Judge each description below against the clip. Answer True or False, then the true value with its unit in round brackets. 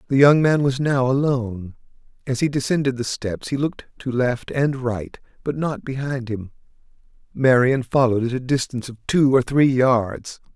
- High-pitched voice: False (130 Hz)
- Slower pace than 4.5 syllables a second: False (5.0 syllables/s)